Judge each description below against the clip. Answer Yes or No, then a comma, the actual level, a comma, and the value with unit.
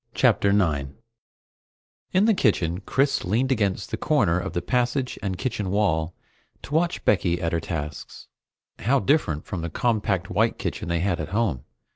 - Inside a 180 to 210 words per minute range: No, average, 165 wpm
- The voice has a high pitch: No, low, 100 Hz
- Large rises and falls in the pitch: Yes, wide, 6.6 semitones